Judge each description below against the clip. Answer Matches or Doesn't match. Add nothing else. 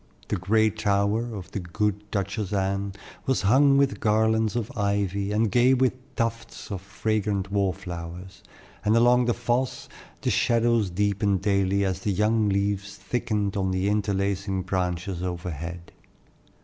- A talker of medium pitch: Doesn't match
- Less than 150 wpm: Matches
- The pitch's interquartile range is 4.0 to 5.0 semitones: Doesn't match